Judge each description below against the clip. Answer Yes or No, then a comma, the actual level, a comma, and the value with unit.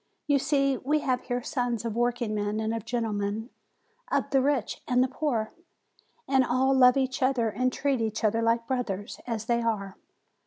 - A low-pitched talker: No, high, 240 Hz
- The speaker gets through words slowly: No, average, 180 wpm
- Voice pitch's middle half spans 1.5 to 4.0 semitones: Yes, average, 2.9 semitones